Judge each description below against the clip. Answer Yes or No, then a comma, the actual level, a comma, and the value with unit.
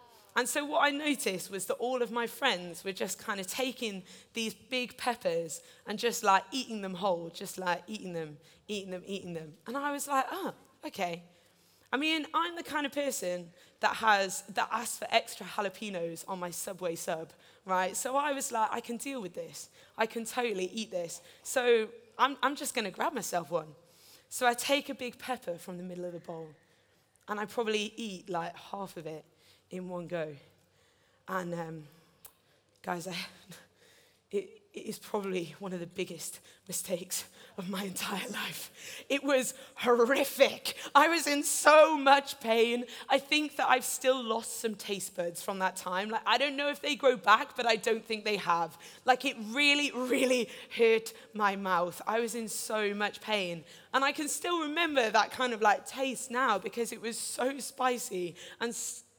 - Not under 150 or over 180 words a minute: No, average, 190 wpm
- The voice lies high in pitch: Yes, high, 220 Hz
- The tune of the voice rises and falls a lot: Yes, wide, 6.0 semitones